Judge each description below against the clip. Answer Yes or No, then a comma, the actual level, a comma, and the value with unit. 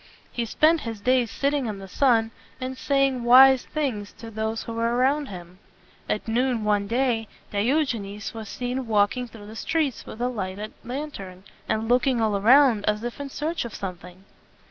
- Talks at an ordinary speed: Yes, average, 190 wpm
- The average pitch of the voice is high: Yes, high, 230 Hz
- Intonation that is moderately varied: Yes, average, 3.8 semitones